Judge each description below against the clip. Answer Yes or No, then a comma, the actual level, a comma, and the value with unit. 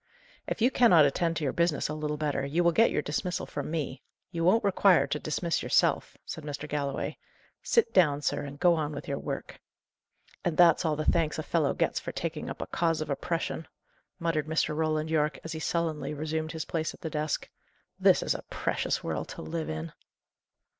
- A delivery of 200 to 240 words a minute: Yes, fast, 205 wpm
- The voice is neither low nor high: Yes, medium, 155 Hz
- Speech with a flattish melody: Yes, narrow, 2.1 semitones